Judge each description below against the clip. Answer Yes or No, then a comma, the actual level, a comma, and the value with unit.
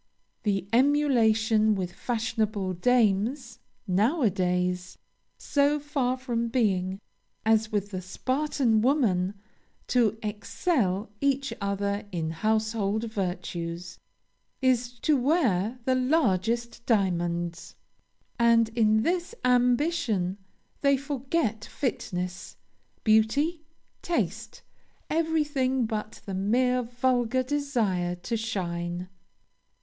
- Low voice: No, high, 225 Hz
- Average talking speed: No, slow, 95 wpm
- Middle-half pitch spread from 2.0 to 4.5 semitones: No, average, 5.0 semitones